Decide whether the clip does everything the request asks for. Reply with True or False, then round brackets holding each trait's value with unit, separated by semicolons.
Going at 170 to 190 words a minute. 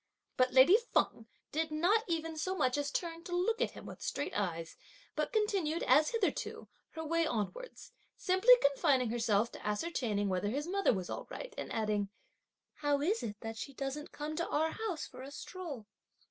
True (185 wpm)